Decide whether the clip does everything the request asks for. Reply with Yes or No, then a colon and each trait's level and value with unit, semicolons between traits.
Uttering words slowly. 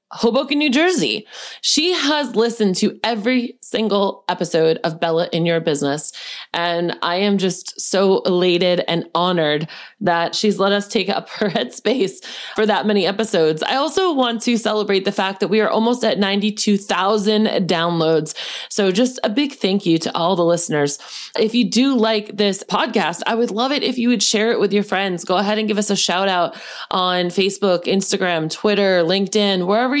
No: average, 180 wpm